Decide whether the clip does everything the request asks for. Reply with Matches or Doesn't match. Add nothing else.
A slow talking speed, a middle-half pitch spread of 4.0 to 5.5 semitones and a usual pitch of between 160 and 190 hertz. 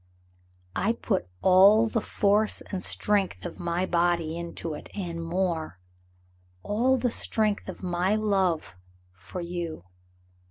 Doesn't match